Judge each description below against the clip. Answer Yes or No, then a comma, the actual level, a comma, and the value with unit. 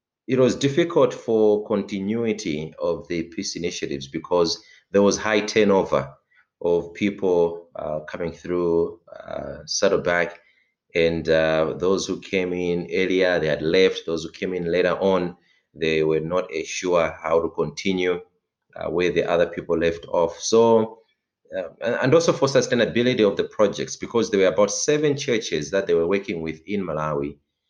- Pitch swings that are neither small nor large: Yes, average, 4.1 semitones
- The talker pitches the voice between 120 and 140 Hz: No, very low, 90 Hz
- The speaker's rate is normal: Yes, average, 160 wpm